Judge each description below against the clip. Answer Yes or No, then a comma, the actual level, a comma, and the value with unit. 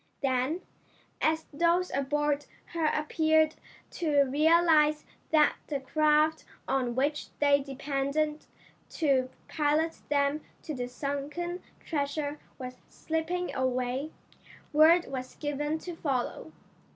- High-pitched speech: Yes, very high, 295 Hz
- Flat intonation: Yes, narrow, 2.3 semitones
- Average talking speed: No, slow, 105 wpm